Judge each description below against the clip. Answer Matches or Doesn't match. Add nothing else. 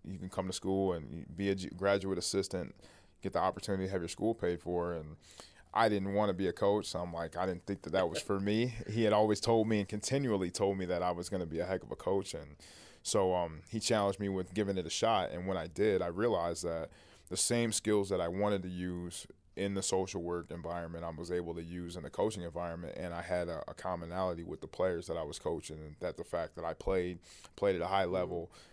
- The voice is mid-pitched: Doesn't match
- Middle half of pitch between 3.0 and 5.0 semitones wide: Doesn't match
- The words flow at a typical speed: Doesn't match